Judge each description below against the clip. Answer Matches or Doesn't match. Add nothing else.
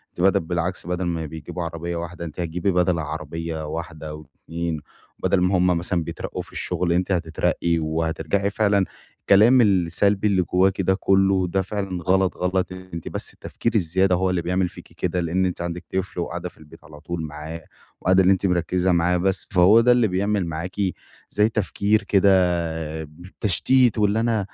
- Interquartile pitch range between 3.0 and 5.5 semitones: Doesn't match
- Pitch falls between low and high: Doesn't match